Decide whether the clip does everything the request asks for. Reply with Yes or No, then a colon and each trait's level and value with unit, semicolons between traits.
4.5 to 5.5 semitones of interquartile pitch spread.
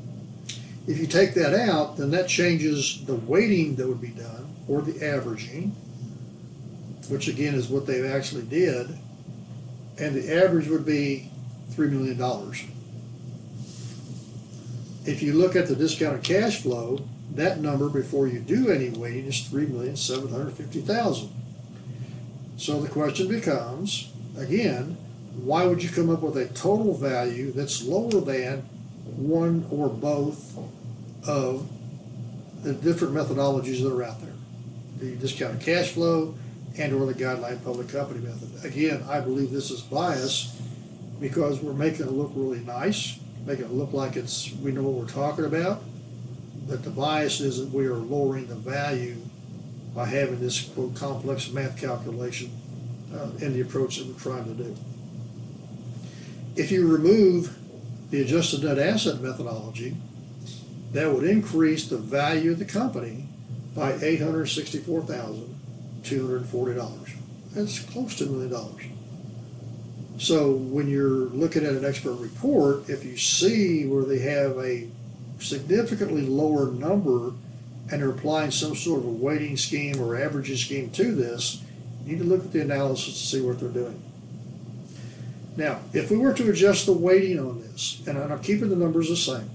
No: average, 3.8 semitones